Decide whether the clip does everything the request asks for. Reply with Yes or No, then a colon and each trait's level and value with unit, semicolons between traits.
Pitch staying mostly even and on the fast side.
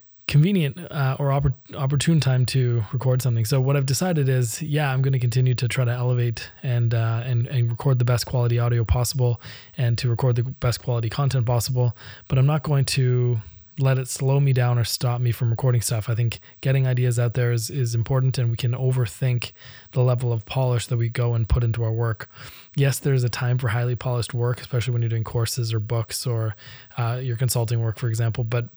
Yes: narrow, 1.9 semitones; fast, 220 wpm